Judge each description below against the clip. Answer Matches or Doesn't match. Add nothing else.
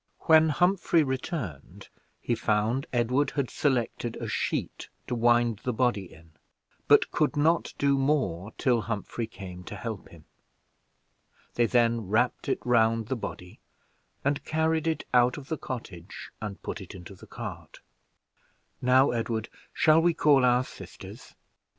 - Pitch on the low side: Matches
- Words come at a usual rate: Matches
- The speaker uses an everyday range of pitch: Matches